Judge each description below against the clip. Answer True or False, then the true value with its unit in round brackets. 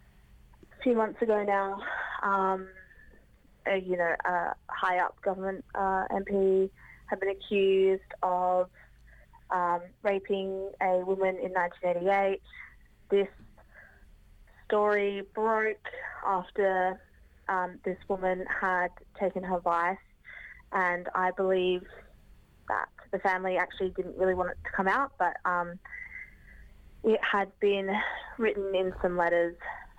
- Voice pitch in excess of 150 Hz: True (190 Hz)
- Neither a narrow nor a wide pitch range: False (1.5 semitones)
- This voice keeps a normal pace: False (115 wpm)